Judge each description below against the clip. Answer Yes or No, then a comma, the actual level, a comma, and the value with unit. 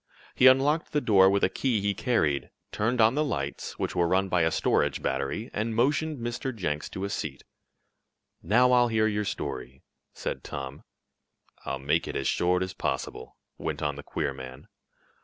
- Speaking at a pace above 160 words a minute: Yes, average, 180 wpm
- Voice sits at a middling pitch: No, low, 100 Hz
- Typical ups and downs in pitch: No, wide, 8.9 semitones